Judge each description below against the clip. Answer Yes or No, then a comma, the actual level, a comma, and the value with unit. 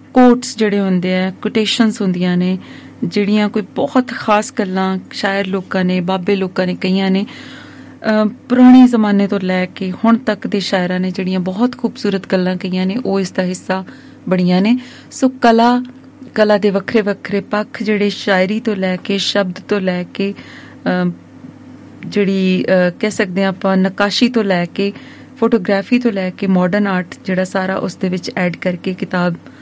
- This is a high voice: Yes, high, 200 Hz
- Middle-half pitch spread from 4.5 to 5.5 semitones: No, average, 3.1 semitones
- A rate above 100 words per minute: Yes, fast, 165 wpm